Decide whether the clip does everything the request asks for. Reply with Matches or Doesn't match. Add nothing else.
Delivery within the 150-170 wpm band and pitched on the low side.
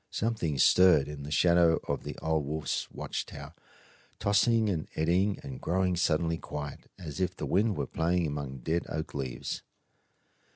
Matches